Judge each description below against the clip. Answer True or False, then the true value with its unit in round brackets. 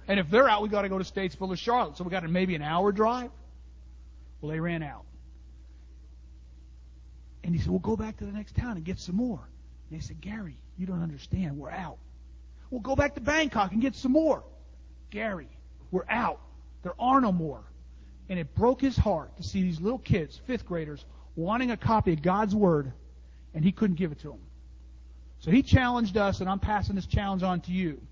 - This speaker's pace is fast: True (215 wpm)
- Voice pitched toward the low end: False (170 Hz)